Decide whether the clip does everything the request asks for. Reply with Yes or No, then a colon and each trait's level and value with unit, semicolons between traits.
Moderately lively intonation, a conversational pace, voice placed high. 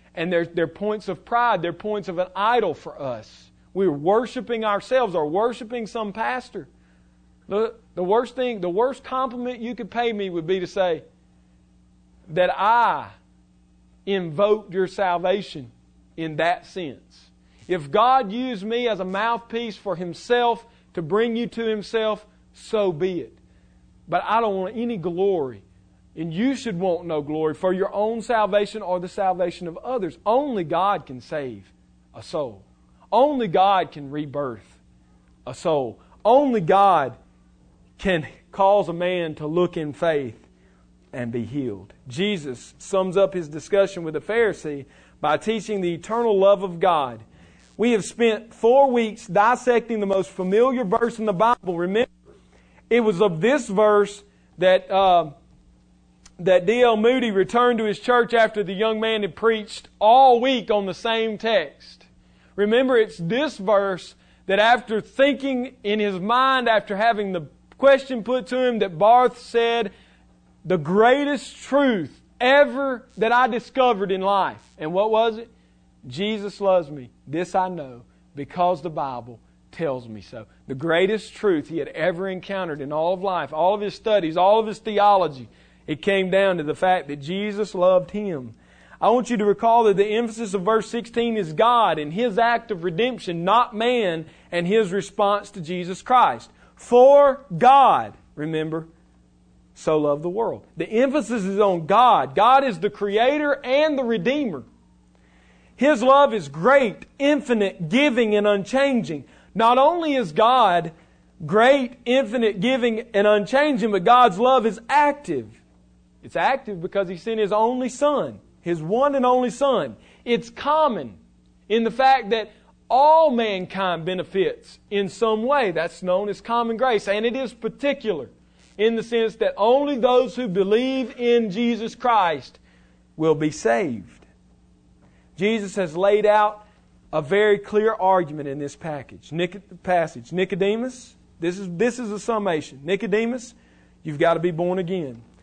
No: wide, 5.8 semitones; average, 155 wpm; high, 200 Hz